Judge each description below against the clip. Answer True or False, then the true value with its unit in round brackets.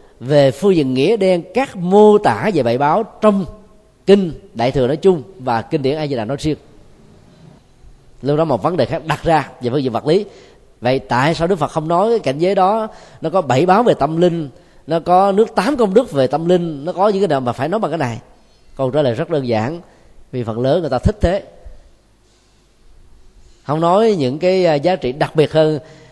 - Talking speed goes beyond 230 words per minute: False (225 wpm)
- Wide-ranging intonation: True (6.1 semitones)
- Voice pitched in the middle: True (155 Hz)